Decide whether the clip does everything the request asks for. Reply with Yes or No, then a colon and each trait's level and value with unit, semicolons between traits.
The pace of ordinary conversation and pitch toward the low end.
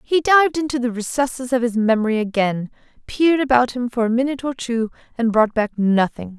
No: average, 195 wpm; high, 240 Hz